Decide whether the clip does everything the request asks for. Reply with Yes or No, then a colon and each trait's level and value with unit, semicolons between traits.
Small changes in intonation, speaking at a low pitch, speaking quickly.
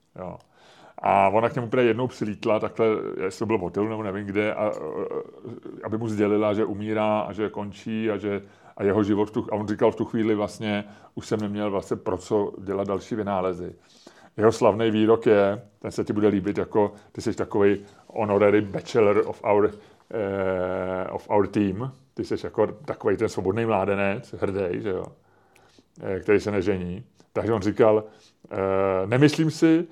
Yes: narrow, 1.9 semitones; low, 105 Hz; fast, 175 wpm